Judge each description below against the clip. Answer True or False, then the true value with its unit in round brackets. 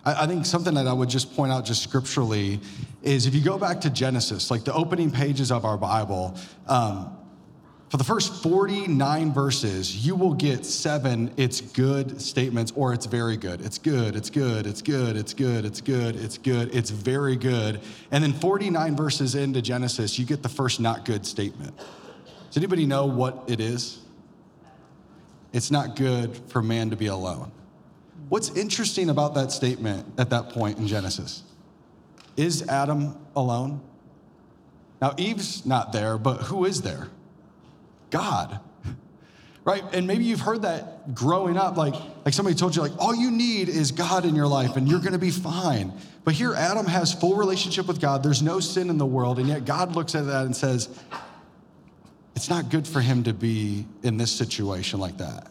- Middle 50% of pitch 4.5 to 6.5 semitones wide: True (5.4 semitones)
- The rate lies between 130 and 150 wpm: False (185 wpm)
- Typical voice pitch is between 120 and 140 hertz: True (135 Hz)